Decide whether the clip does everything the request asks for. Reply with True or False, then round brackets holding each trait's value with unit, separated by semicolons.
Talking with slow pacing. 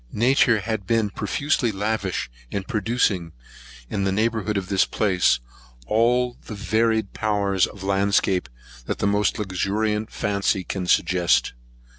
True (130 wpm)